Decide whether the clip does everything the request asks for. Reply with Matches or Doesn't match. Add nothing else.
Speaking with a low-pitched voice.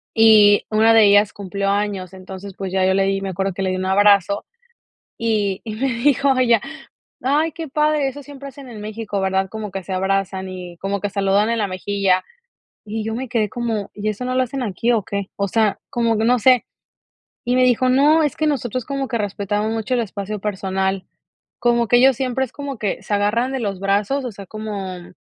Doesn't match